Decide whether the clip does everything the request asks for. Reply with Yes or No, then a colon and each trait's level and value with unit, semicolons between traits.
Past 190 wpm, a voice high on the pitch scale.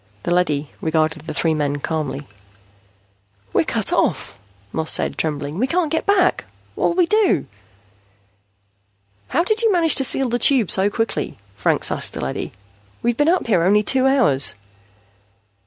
No: average, 155 wpm; high, 210 Hz